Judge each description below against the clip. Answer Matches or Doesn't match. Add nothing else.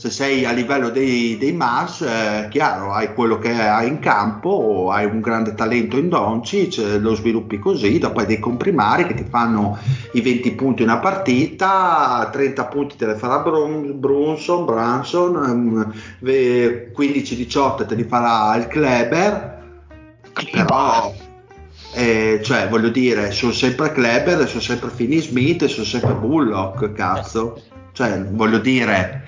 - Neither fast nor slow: Matches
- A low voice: Matches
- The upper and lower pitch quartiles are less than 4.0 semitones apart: Matches